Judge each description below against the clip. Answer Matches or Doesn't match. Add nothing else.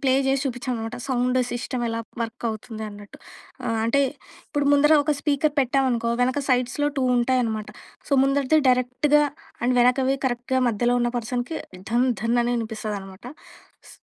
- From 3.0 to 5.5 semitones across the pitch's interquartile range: Doesn't match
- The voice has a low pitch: Doesn't match